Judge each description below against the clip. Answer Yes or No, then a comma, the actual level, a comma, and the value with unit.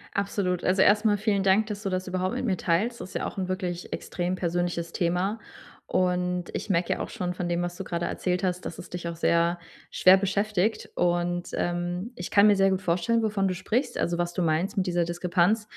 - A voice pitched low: No, medium, 185 Hz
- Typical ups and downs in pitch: No, narrow, 2.3 semitones